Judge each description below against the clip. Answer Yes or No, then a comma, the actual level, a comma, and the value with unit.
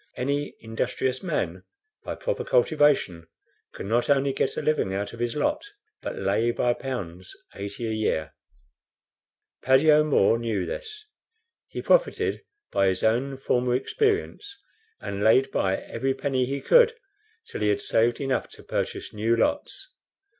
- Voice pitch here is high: No, low, 125 Hz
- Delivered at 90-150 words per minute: Yes, average, 145 wpm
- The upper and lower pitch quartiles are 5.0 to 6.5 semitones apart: Yes, wide, 5.4 semitones